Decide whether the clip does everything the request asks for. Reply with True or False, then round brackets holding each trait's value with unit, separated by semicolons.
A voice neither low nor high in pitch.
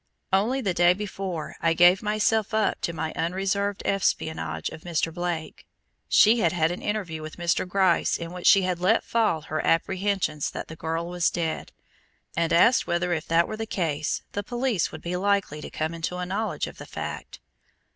True (180 Hz)